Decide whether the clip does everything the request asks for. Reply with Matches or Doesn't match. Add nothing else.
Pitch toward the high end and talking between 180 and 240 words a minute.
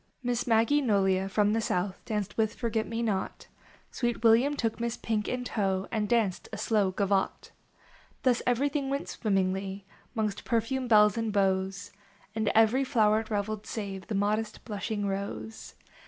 Doesn't match